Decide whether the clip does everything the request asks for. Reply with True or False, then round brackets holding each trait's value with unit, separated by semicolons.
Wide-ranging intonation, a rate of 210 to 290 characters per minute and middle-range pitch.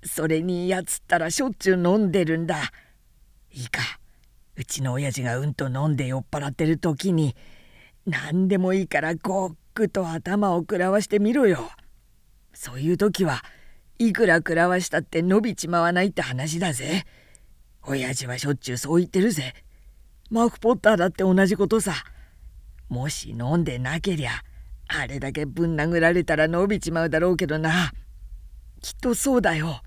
False (5.8 semitones; 325 characters per minute; 165 Hz)